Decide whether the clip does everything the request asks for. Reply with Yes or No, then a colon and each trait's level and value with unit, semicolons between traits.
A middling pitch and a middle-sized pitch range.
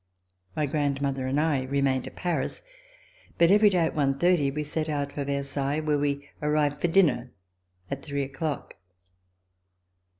No: medium, 145 Hz; narrow, 2.0 semitones